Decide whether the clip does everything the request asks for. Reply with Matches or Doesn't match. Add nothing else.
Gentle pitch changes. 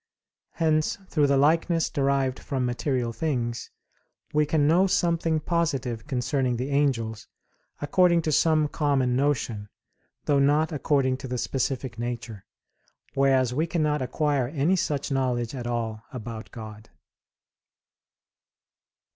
Doesn't match